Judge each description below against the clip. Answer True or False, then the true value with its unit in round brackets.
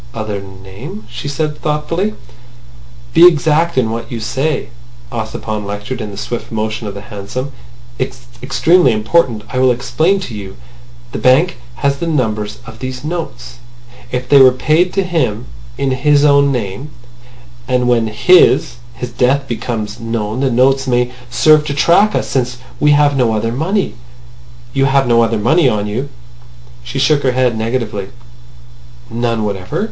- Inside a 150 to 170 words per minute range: True (160 wpm)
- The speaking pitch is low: True (125 Hz)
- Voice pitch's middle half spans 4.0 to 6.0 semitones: True (4.3 semitones)